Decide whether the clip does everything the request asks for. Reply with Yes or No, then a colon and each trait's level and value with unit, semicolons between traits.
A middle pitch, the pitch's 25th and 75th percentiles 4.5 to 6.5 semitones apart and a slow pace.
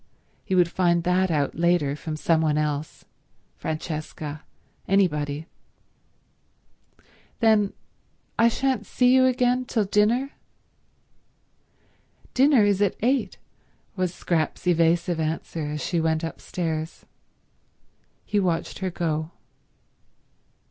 Yes: medium, 175 Hz; average, 4.8 semitones; slow, 100 wpm